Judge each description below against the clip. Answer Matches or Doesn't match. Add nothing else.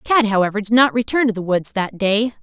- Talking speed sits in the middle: Doesn't match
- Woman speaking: Matches